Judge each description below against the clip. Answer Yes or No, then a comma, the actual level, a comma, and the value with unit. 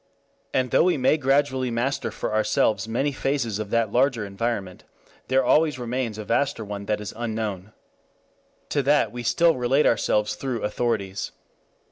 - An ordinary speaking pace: Yes, average, 155 wpm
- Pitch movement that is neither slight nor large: Yes, average, 4.0 semitones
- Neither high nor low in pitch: No, low, 120 Hz